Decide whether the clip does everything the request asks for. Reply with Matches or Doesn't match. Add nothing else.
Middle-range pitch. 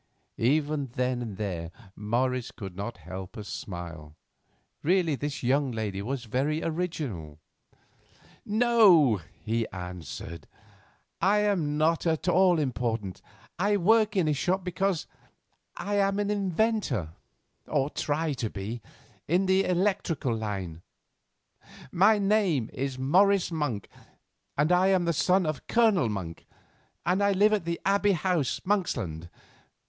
Matches